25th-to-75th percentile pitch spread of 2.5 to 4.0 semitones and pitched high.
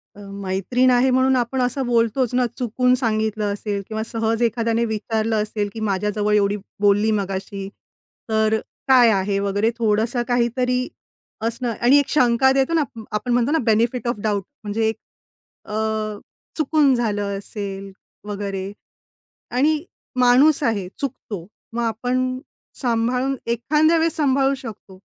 Yes: average, 3.4 semitones; high, 230 Hz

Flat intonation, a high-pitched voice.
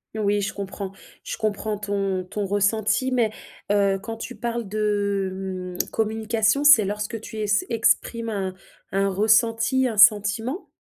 Yes: narrow, 2.1 semitones; high, 210 Hz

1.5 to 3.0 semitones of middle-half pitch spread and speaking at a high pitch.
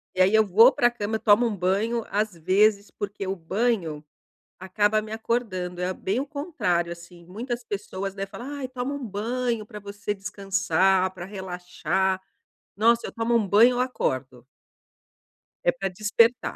No: average, 3.8 semitones; high, 205 Hz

